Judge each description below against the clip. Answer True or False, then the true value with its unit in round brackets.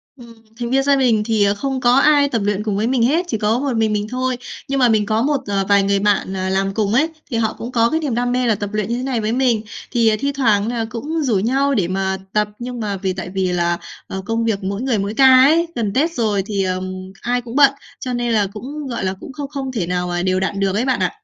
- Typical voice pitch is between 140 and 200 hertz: False (225 Hz)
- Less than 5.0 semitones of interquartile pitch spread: True (4.3 semitones)